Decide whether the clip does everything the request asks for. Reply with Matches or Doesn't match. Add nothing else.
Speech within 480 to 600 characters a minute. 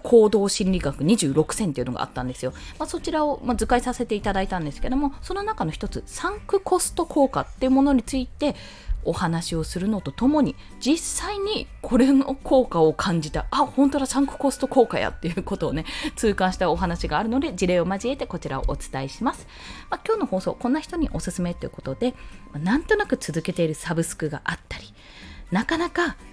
Doesn't match